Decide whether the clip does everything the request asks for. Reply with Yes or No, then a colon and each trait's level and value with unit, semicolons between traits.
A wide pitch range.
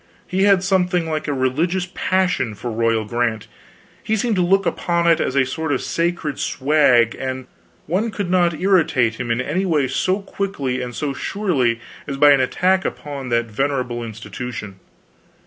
Yes: wide, 6.5 semitones